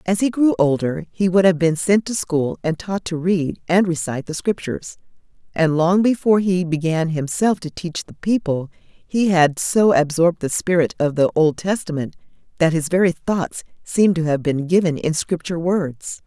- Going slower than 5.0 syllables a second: Yes, 4.8 syllables/s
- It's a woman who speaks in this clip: Yes, female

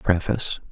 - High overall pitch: No, very low, 95 Hz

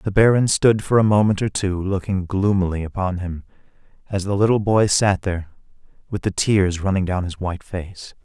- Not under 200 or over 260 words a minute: No, average, 190 wpm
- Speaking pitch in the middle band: No, very low, 95 Hz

